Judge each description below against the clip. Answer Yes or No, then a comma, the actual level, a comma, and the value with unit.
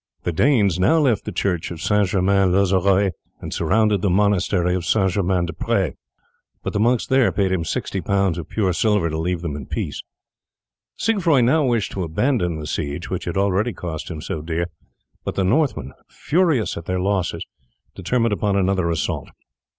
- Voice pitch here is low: Yes, very low, 95 Hz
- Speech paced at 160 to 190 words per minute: Yes, average, 180 wpm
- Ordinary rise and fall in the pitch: Yes, average, 3.7 semitones